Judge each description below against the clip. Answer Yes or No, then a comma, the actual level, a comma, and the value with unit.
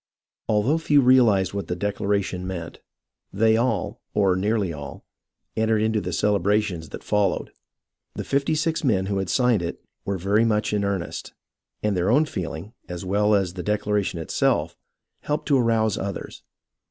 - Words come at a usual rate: Yes, average, 165 wpm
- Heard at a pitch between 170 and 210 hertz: No, low, 105 Hz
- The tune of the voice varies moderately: Yes, average, 3.0 semitones